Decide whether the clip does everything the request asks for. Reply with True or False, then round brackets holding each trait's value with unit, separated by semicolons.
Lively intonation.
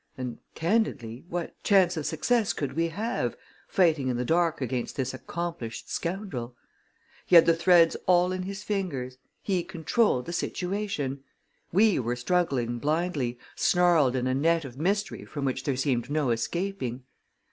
True (5.8 semitones)